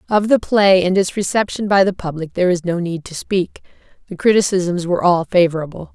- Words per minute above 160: Yes, average, 200 wpm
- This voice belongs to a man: No, female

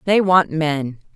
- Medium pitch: Yes, medium, 160 Hz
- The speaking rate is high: No, average, 155 wpm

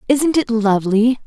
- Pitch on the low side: No, high, 235 Hz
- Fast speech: No, average, 145 wpm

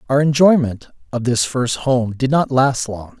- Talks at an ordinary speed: Yes, average, 190 wpm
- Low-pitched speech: Yes, low, 130 Hz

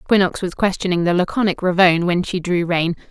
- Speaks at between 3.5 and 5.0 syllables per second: No, 6.1 syllables/s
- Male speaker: No, female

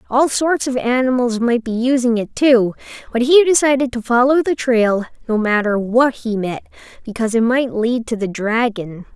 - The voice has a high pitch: Yes, high, 240 Hz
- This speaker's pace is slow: No, average, 185 wpm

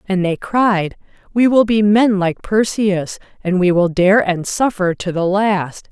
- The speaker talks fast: No, average, 185 wpm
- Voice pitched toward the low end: No, high, 195 Hz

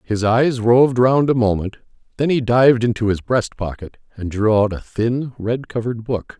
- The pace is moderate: Yes, average, 195 wpm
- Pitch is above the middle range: No, low, 115 Hz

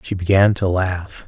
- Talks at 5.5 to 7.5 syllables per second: No, 4.3 syllables/s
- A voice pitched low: Yes, very low, 95 Hz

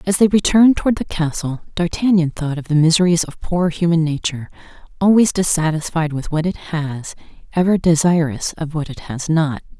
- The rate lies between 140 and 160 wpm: No, average, 170 wpm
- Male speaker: No, female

